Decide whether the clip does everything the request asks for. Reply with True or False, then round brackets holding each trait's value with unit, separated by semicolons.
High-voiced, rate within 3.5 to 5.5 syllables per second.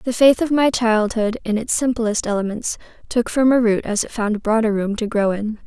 True (225 Hz; 5.0 syllables/s)